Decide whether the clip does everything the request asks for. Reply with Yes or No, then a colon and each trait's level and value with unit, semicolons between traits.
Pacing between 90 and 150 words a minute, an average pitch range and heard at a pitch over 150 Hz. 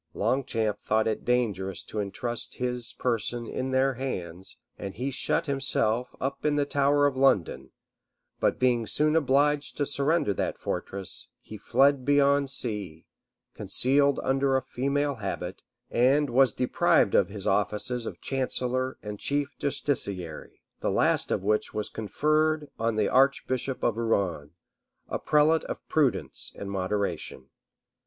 No: average, 140 wpm; average, 4.8 semitones; low, 125 Hz